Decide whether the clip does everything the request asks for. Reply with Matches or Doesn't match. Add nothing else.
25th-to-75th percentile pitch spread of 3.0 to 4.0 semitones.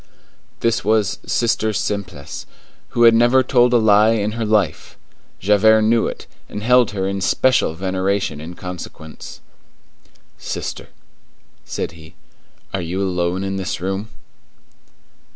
Matches